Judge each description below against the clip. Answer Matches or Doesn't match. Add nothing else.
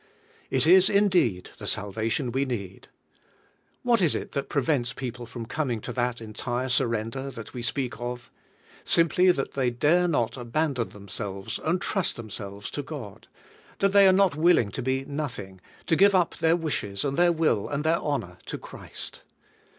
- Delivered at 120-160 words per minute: Doesn't match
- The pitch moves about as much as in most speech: Doesn't match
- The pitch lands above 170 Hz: Doesn't match